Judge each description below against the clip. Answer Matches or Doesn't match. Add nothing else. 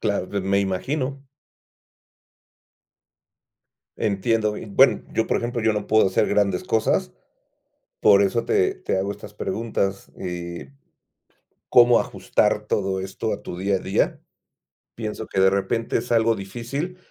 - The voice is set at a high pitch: Doesn't match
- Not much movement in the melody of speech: Doesn't match